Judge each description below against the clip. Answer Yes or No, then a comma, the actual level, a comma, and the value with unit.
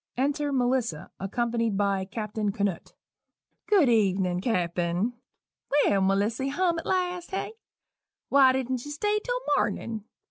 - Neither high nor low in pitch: No, high, 235 Hz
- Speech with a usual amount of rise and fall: No, wide, 6.6 semitones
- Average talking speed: No, slow, 130 wpm